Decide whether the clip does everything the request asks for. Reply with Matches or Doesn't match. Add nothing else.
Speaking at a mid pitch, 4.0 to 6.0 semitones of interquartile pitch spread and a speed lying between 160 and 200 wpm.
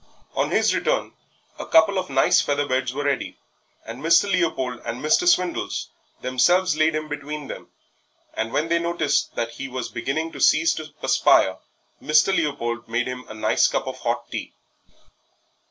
Matches